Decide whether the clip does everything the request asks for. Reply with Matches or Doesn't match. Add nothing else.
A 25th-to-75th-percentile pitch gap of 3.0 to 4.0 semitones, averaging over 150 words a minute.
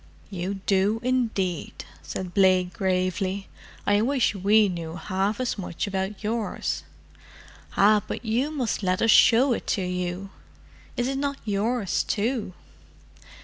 Doesn't match